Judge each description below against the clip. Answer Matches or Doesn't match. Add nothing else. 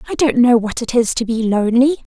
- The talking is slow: Doesn't match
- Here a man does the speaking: Doesn't match